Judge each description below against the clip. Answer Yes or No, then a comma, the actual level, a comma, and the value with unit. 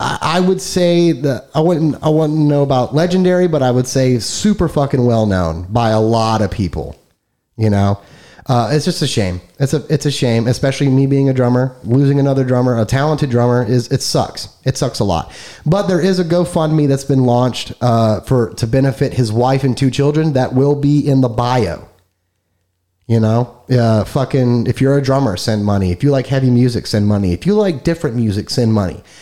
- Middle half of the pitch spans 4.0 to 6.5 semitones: Yes, average, 4.5 semitones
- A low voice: Yes, low, 130 Hz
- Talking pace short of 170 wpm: No, fast, 205 wpm